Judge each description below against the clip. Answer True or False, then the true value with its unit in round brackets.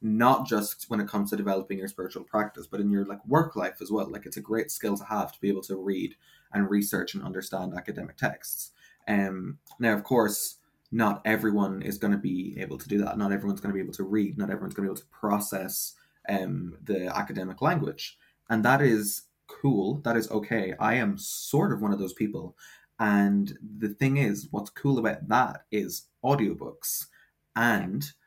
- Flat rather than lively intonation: True (1.8 semitones)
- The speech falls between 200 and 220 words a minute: True (205 wpm)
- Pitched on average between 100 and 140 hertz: True (105 Hz)